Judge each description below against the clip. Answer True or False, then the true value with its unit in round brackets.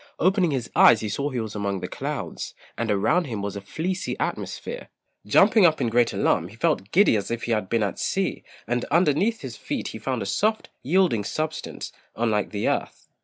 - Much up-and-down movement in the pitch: True (8.1 semitones)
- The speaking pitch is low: True (120 Hz)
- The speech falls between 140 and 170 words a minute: False (205 wpm)